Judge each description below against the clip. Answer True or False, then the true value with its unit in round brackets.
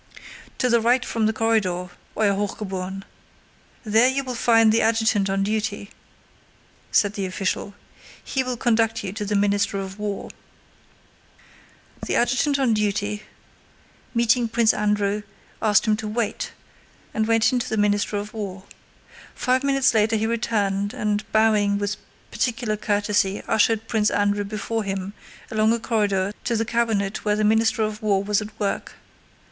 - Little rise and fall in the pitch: True (1.9 semitones)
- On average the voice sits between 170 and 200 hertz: False (215 Hz)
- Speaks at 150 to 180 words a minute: True (155 wpm)